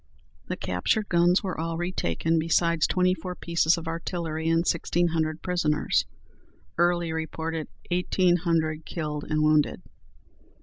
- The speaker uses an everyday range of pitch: No, narrow, 1.7 semitones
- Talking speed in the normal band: No, slow, 130 wpm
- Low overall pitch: No, medium, 165 Hz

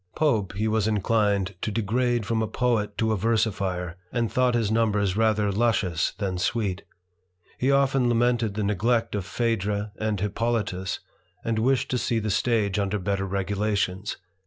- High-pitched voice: No, low, 110 Hz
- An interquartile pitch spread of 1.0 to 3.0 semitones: Yes, narrow, 2.6 semitones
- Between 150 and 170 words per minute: Yes, average, 160 wpm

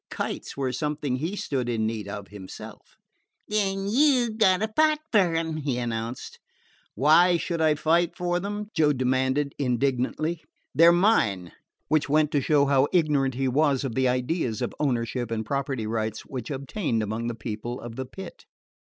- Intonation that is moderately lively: No, wide, 5.8 semitones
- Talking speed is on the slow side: No, average, 175 wpm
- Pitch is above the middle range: No, medium, 140 Hz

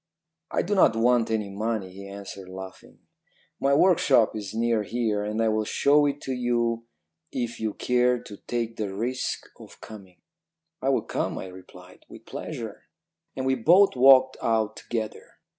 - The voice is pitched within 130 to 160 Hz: No, low, 115 Hz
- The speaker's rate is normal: Yes, average, 165 wpm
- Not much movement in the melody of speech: No, average, 3.5 semitones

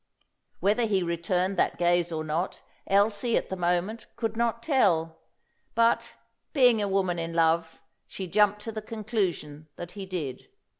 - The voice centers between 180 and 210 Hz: Yes, high, 190 Hz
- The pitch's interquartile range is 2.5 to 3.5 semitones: No, average, 4.2 semitones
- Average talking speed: Yes, average, 155 wpm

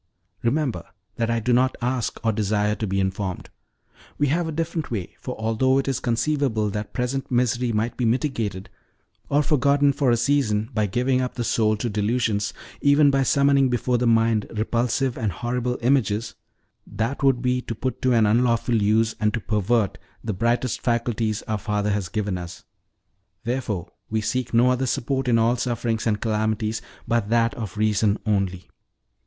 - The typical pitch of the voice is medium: No, low, 115 Hz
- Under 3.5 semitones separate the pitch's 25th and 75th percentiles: Yes, average, 3.0 semitones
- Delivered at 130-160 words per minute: No, average, 175 wpm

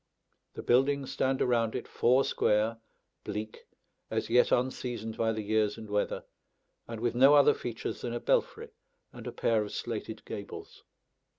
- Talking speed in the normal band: Yes, average, 160 wpm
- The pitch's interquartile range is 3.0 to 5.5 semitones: No, narrow, 2.5 semitones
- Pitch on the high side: No, low, 115 Hz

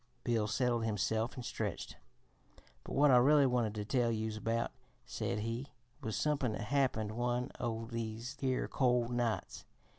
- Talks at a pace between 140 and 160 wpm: Yes, average, 155 wpm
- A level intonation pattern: Yes, narrow, 2.2 semitones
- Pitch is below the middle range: Yes, low, 120 Hz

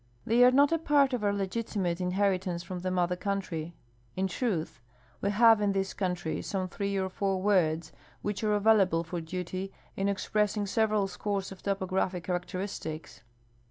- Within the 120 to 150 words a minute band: No, average, 170 wpm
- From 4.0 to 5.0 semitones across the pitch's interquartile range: No, narrow, 2.4 semitones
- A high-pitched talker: Yes, high, 195 Hz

